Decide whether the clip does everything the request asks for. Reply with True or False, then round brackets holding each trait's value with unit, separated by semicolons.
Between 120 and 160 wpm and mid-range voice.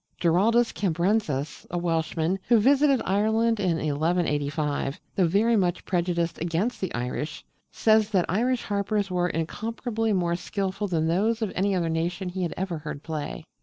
True (155 wpm; 180 Hz)